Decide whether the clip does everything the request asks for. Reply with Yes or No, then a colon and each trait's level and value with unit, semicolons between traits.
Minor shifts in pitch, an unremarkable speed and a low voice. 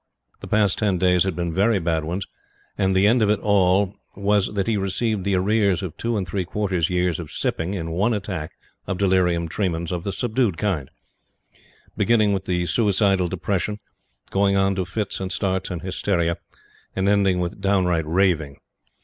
Yes: narrow, 2.3 semitones; average, 175 wpm; very low, 95 Hz